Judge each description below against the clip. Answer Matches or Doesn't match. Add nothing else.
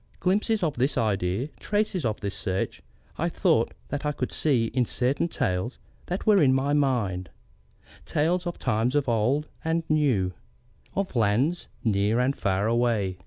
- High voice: Doesn't match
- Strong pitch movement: Matches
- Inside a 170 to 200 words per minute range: Doesn't match